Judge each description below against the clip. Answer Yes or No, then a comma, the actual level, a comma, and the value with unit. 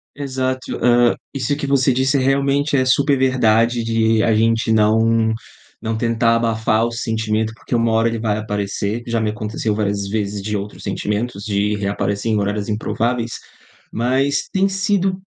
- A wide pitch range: No, average, 3.2 semitones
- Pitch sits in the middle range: No, low, 115 Hz